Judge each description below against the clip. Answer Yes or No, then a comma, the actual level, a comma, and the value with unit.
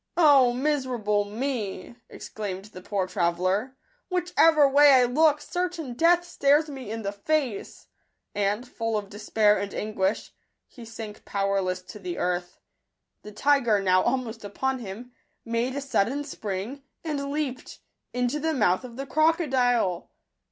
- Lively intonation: Yes, wide, 5.7 semitones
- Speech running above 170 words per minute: No, average, 155 wpm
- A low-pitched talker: No, high, 240 Hz